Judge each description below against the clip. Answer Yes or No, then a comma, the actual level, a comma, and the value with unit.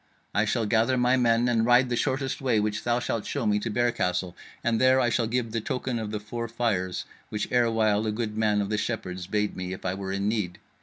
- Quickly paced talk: Yes, fast, 245 wpm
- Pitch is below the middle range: Yes, low, 110 Hz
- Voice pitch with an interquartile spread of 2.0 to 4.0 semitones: Yes, narrow, 2.6 semitones